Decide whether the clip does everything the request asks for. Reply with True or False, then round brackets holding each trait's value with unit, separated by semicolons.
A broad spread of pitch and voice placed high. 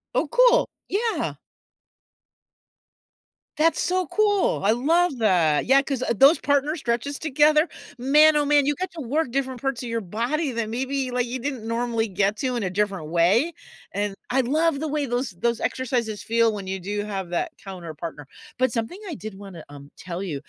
True (6.0 semitones; 245 Hz)